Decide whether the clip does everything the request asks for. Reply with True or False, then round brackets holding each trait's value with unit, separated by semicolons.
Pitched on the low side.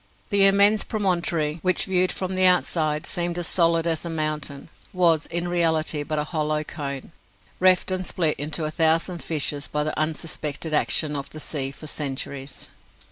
False (160 Hz)